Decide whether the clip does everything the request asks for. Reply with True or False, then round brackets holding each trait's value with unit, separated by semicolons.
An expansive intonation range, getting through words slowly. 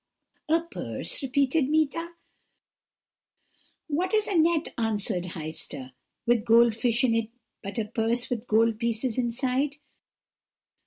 False (4.9 semitones; 120 wpm)